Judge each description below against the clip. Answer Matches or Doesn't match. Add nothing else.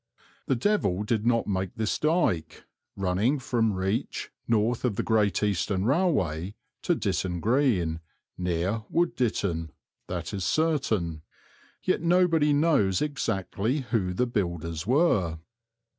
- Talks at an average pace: Doesn't match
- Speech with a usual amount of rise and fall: Doesn't match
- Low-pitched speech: Matches